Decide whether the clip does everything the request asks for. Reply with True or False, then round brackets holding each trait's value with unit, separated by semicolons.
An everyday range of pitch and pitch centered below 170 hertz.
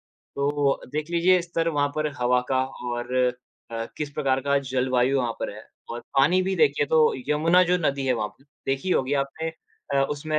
True (3.2 semitones; 140 Hz)